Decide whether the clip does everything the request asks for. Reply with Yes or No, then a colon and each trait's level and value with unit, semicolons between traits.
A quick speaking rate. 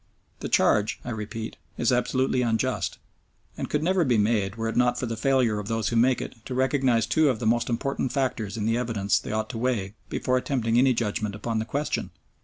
Yes: fast, 215 wpm